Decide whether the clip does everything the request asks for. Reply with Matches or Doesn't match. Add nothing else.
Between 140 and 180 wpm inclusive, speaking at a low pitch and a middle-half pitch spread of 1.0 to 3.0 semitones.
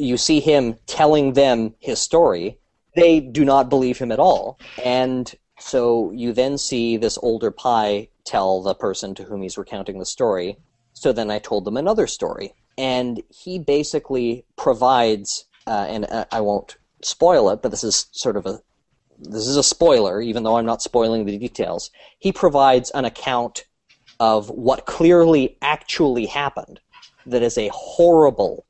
Doesn't match